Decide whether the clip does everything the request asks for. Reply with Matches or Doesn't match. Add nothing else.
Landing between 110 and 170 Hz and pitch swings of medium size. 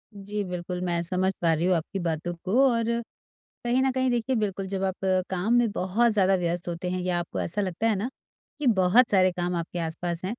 Doesn't match